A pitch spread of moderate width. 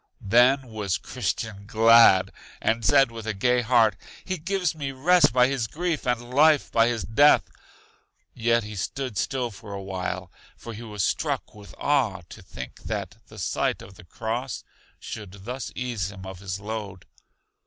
Yes: average, 4.3 semitones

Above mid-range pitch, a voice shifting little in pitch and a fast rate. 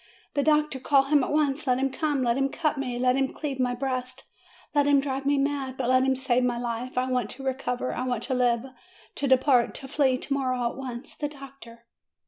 Yes: very high, 265 Hz; narrow, 1.8 semitones; fast, 230 wpm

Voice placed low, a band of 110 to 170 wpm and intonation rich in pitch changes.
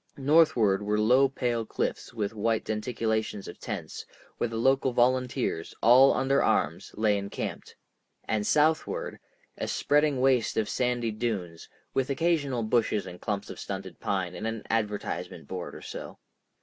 No: low, 115 Hz; average, 150 wpm; average, 4.2 semitones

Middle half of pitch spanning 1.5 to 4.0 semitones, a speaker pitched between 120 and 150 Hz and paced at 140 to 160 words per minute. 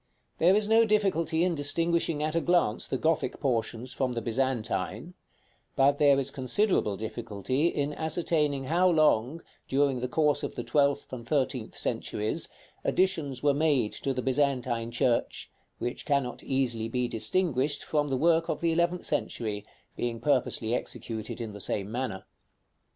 No: average, 4.9 semitones; medium, 140 Hz; average, 155 wpm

